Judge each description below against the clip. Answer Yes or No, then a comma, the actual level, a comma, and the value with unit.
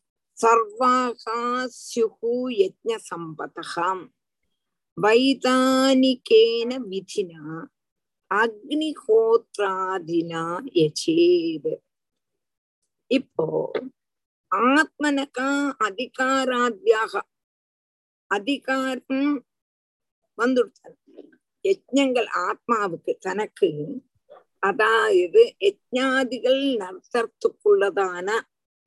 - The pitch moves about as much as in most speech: No, wide, 5.8 semitones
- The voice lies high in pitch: Yes, very high, 255 Hz